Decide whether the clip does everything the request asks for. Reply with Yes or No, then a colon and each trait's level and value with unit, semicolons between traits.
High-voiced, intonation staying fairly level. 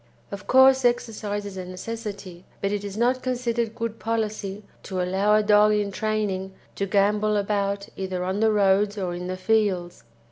Yes: high, 205 Hz; narrow, 2.3 semitones